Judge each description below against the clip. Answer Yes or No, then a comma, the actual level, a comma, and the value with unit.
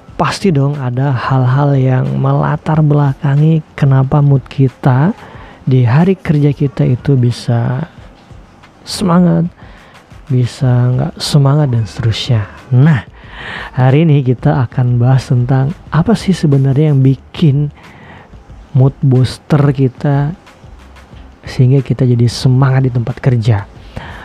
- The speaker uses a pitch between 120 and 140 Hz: Yes, low, 135 Hz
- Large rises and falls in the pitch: No, average, 2.9 semitones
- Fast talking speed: No, average, 110 wpm